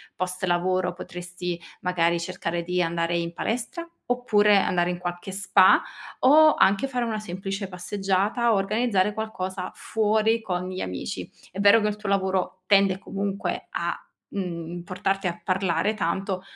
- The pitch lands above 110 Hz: Yes, high, 190 Hz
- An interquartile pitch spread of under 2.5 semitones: No, average, 2.8 semitones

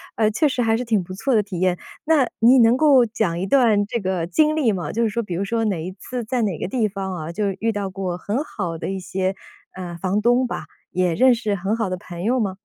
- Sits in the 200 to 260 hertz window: Yes, high, 205 Hz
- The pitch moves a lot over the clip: No, average, 4.1 semitones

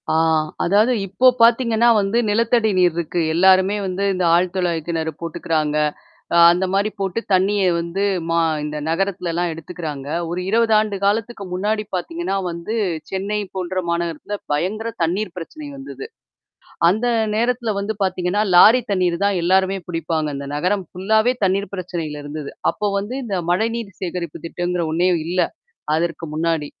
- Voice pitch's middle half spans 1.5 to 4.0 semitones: Yes, average, 3.7 semitones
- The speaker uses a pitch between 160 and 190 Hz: Yes, medium, 185 Hz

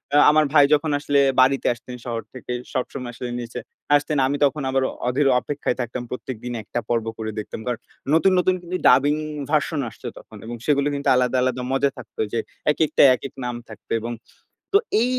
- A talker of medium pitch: No, low, 130 Hz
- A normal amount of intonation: Yes, average, 3.2 semitones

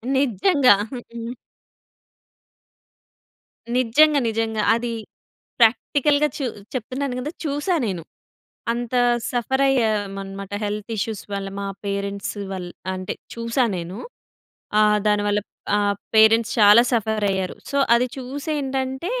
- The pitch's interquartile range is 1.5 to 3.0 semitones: No, average, 4.4 semitones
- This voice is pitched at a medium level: No, high, 225 Hz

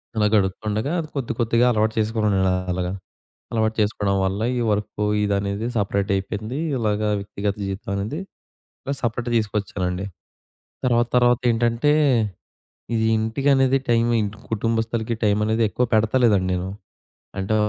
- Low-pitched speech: Yes, low, 110 Hz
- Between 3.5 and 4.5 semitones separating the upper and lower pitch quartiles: No, average, 2.8 semitones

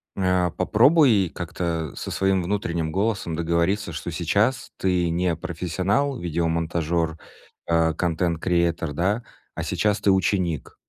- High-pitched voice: No, very low, 85 Hz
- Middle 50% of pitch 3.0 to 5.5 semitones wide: No, narrow, 2.6 semitones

